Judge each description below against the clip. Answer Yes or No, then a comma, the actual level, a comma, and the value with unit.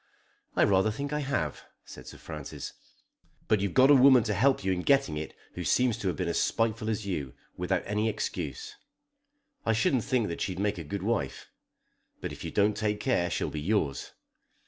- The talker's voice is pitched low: Yes, low, 105 Hz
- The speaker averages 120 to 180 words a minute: No, average, 200 wpm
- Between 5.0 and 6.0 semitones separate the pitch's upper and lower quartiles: Yes, wide, 5.4 semitones